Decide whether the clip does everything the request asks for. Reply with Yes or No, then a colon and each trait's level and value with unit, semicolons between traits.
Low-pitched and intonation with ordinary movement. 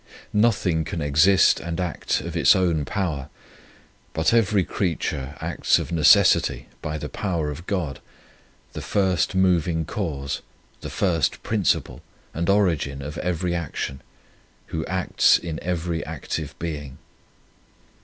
Yes: very low, 85 Hz; average, 3.5 semitones